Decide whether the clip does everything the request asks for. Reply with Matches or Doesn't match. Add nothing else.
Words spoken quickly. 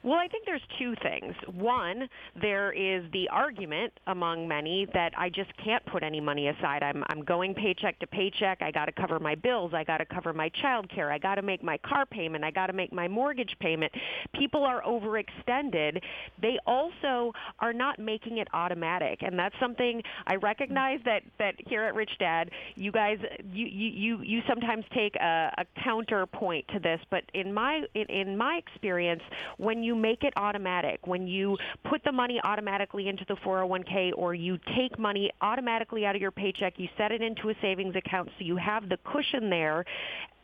Doesn't match